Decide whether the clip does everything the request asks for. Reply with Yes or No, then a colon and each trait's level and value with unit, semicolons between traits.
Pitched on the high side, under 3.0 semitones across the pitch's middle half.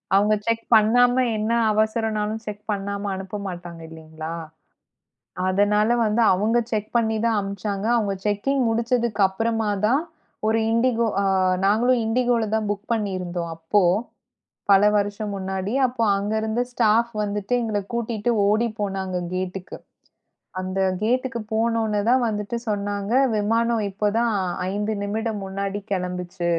Yes: high, 210 Hz; narrow, 2.4 semitones